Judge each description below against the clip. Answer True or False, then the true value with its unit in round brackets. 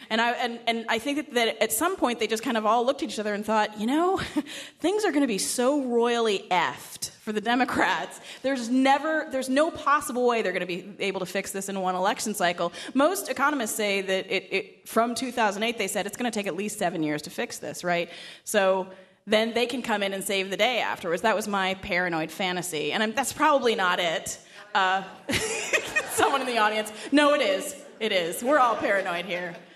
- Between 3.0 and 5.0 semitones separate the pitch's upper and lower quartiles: False (5.5 semitones)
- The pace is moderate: False (220 wpm)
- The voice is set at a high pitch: True (220 Hz)